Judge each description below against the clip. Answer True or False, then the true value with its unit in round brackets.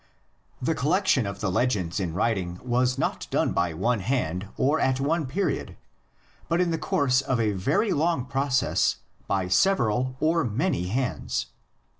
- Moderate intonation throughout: False (6.9 semitones)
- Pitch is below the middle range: True (125 Hz)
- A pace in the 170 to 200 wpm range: False (155 wpm)